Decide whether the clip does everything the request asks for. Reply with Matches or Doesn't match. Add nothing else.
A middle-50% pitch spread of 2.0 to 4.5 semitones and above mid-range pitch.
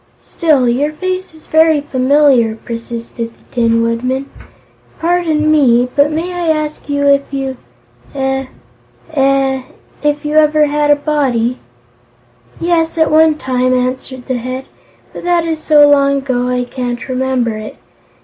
Matches